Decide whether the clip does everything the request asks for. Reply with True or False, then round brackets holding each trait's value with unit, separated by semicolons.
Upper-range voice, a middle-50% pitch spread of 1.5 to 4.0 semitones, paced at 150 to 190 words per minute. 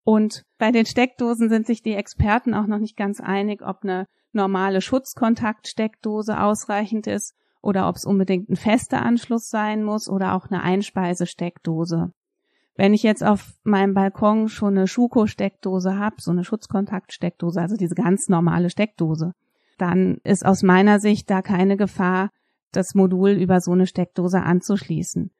True (200 Hz; 2.7 semitones; 155 wpm)